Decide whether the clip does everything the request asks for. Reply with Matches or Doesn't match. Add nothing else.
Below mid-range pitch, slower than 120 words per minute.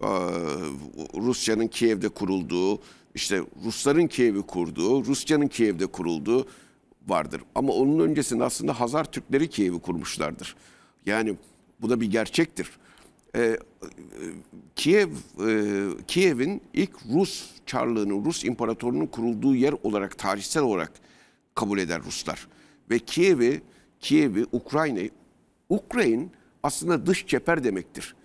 Matches